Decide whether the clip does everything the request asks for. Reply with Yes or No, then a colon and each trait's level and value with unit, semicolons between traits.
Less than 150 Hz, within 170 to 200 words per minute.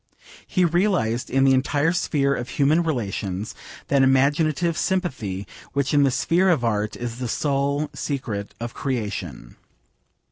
No: low, 135 Hz; average, 140 wpm